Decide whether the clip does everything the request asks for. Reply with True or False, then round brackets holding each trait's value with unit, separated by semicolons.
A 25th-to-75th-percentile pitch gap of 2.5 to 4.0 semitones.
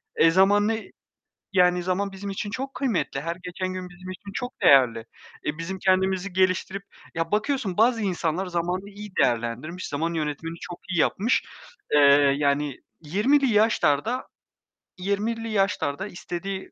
True (3.6 semitones)